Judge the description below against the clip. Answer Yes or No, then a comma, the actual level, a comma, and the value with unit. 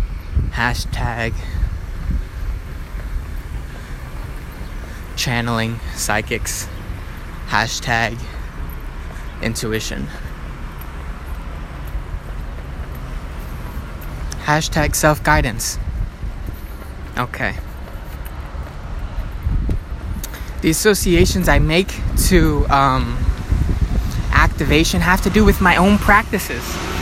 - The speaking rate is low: Yes, slow, 50 wpm